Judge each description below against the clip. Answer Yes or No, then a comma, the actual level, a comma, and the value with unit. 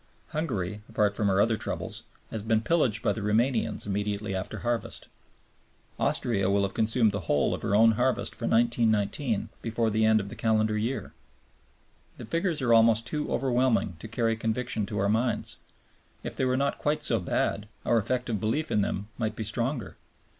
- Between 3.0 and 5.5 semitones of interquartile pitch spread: No, narrow, 2.6 semitones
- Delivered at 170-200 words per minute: Yes, average, 180 wpm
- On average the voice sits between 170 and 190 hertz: No, low, 110 Hz